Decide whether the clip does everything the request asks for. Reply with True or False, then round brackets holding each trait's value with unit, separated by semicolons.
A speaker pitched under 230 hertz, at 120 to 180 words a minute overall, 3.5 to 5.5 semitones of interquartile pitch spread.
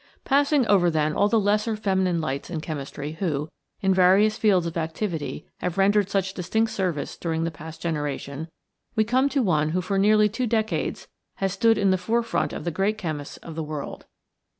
False (185 Hz; 190 wpm; 4.8 semitones)